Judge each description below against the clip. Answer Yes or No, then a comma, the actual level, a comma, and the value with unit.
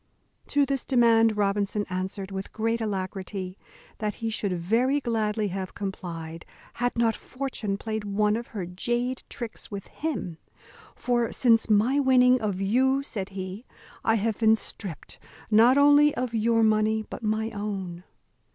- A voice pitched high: Yes, high, 220 Hz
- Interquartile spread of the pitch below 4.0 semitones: Yes, average, 3.3 semitones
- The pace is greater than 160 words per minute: No, average, 150 wpm